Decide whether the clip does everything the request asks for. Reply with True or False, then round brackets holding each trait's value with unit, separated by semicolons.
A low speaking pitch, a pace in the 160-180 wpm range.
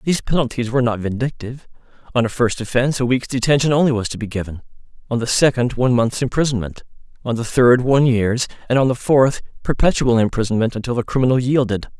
False (125 Hz; 190 wpm)